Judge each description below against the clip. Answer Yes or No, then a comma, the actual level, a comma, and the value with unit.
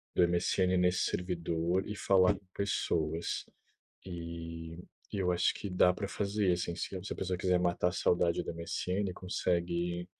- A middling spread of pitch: No, narrow, 1.5 semitones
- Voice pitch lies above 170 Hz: No, very low, 90 Hz